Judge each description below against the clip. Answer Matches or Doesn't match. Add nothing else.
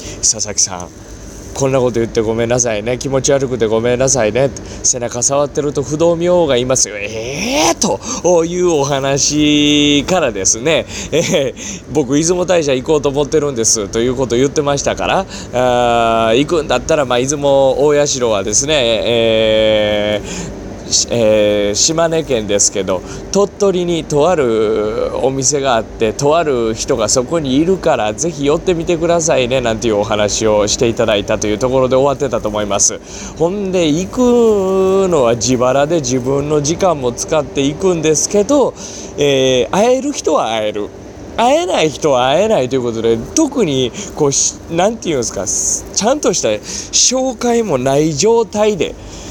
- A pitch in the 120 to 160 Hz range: Matches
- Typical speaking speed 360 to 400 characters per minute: Doesn't match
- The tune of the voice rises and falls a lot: Matches